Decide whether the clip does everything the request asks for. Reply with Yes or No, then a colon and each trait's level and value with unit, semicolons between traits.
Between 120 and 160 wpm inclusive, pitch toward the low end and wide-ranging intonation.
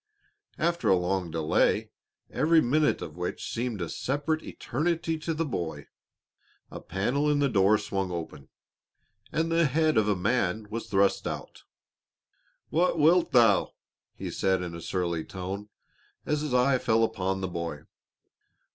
Yes: average, 150 wpm; low, 110 Hz; wide, 8.5 semitones